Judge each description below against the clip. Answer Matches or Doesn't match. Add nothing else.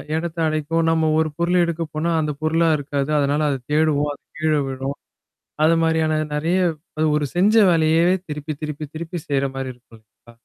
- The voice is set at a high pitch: Doesn't match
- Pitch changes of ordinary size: Doesn't match